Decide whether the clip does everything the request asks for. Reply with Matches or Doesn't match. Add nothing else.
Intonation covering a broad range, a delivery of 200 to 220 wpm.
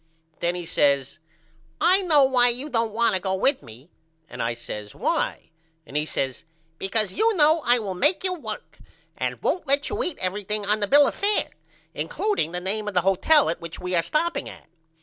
Matches